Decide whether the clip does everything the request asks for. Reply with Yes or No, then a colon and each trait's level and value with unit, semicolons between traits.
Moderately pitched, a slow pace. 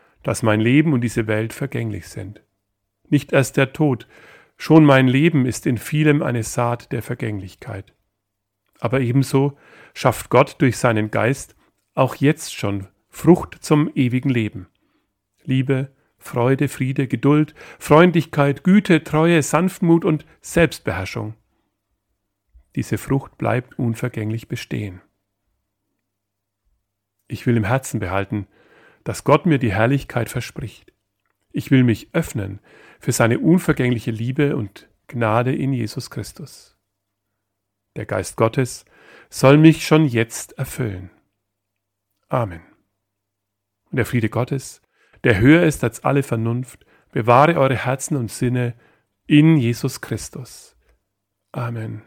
No: low, 120 Hz; slow, 120 wpm